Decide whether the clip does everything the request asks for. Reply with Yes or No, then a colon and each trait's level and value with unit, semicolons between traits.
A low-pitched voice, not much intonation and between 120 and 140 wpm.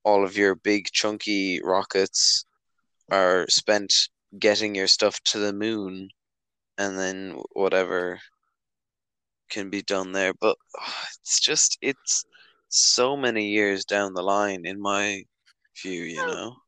Yes: low, 100 Hz; narrow, 1.5 semitones; slow, 135 wpm